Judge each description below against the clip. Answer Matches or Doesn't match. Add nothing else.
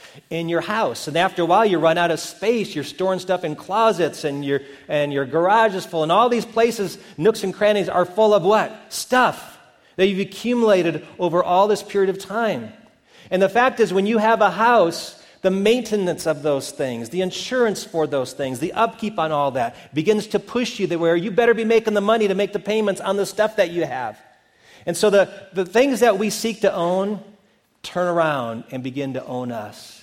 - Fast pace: Matches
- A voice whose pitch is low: Doesn't match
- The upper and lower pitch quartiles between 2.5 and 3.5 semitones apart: Doesn't match